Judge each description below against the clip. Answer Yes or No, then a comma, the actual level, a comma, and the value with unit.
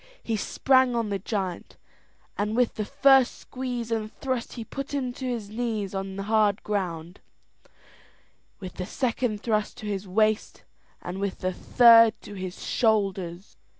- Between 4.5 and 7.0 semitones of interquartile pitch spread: No, average, 3.5 semitones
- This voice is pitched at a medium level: No, high, 215 Hz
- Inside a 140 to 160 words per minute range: Yes, average, 155 wpm